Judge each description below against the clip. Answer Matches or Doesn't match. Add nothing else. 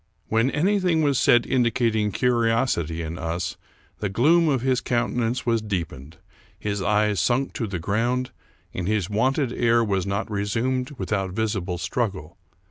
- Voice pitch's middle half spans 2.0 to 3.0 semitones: Doesn't match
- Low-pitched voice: Matches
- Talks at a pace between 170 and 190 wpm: Doesn't match